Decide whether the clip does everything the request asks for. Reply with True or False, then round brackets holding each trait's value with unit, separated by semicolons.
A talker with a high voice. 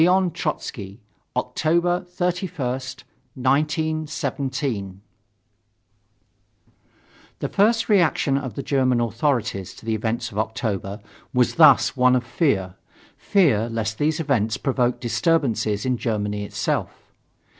False (130 Hz)